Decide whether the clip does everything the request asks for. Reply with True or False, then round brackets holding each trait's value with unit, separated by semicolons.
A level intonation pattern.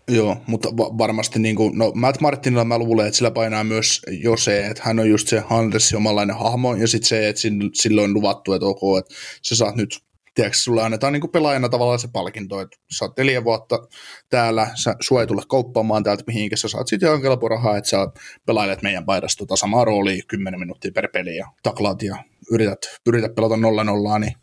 True (2.1 semitones)